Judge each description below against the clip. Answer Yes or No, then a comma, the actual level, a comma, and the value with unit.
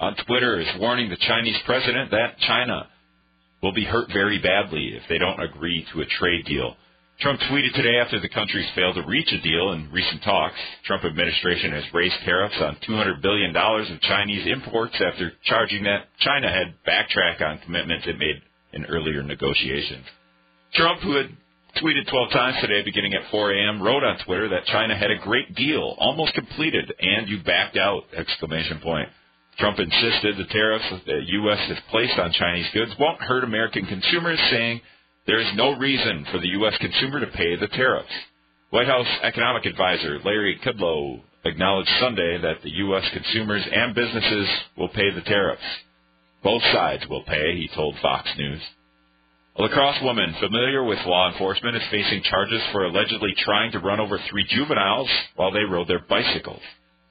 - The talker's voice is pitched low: Yes, very low, 95 Hz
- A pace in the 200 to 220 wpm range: No, average, 175 wpm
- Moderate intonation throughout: No, wide, 7.0 semitones